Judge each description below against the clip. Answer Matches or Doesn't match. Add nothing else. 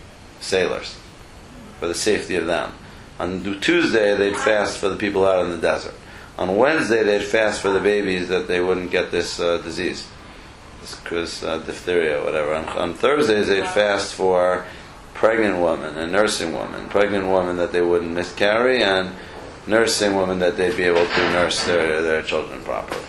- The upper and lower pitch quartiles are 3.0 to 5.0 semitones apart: Doesn't match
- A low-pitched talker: Matches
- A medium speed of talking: Matches